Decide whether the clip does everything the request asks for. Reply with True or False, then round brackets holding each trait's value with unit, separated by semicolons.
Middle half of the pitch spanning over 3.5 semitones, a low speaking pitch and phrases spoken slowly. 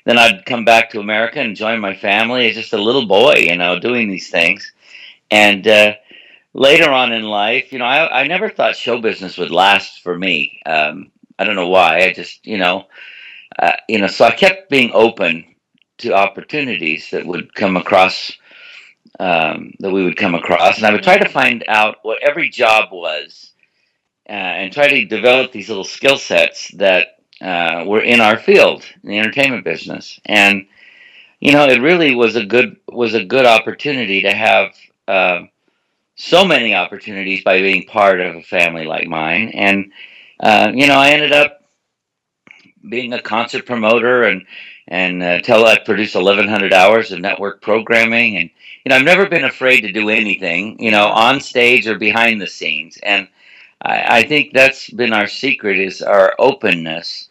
False (4.1 semitones; 110 Hz; 185 wpm)